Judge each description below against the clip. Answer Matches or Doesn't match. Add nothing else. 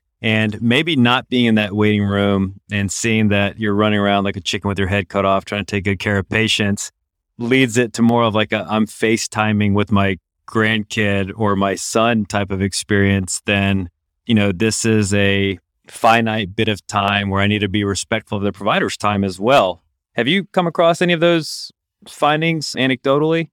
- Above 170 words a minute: Matches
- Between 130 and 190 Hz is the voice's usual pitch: Doesn't match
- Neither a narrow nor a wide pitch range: Doesn't match